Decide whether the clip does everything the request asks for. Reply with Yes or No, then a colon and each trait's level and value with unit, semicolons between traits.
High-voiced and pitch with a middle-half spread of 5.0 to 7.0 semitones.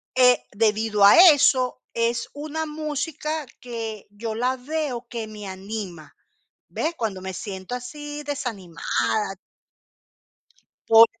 Yes: high, 230 Hz; wide, 5.6 semitones